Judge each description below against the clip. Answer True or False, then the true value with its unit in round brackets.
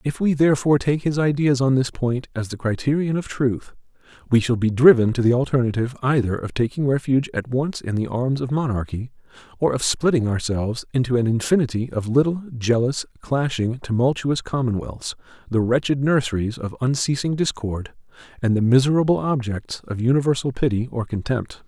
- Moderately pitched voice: False (125 Hz)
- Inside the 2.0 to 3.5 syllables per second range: False (5.6 syllables/s)